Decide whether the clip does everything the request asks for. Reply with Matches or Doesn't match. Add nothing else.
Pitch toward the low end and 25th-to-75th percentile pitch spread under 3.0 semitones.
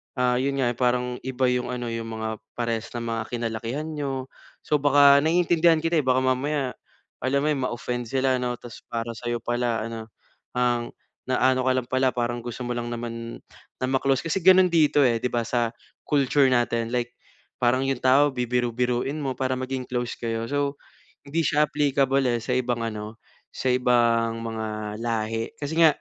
Matches